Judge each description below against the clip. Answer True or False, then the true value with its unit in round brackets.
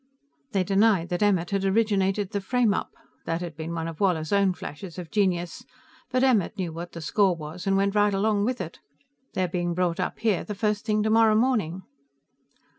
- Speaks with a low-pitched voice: False (195 Hz)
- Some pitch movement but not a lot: True (3.3 semitones)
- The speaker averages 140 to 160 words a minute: False (190 wpm)